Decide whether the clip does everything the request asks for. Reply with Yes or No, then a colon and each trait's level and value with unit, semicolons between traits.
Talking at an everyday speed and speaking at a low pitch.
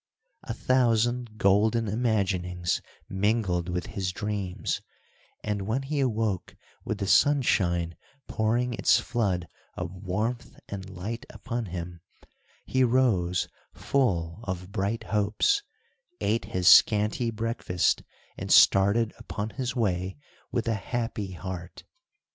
No: slow, 115 wpm; low, 105 Hz